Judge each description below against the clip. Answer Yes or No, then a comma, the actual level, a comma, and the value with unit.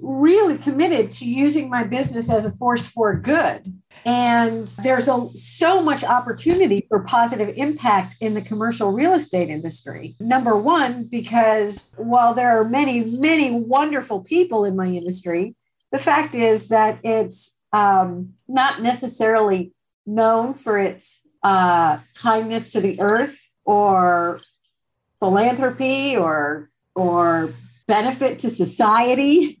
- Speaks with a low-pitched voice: No, high, 225 Hz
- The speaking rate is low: Yes, slow, 125 wpm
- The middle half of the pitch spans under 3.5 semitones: No, average, 4.7 semitones